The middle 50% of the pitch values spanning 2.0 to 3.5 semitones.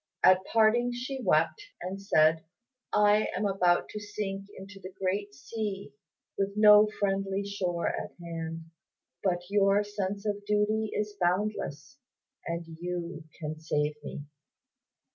Yes: average, 3.0 semitones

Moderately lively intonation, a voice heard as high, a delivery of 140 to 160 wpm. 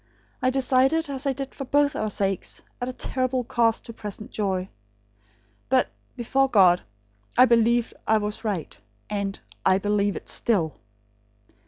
Yes: average, 4.2 semitones; high, 230 Hz; average, 145 wpm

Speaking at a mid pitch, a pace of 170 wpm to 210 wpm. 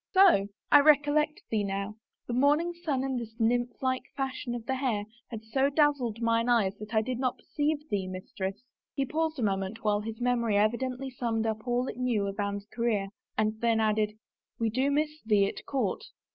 No: high, 235 Hz; average, 200 wpm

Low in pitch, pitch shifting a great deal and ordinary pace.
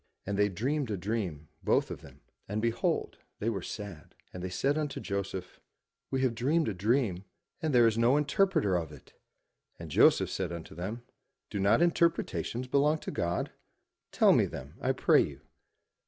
Yes: low, 110 Hz; wide, 6.6 semitones; average, 175 wpm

